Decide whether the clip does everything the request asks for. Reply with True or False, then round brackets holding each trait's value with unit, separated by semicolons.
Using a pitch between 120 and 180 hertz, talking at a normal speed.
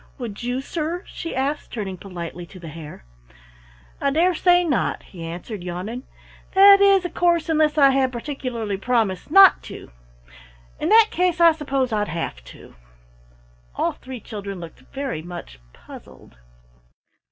False (255 Hz; 150 wpm)